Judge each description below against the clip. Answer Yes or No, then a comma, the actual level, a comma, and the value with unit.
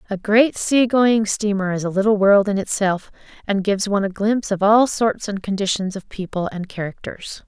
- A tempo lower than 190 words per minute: No, average, 200 wpm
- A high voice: Yes, high, 205 Hz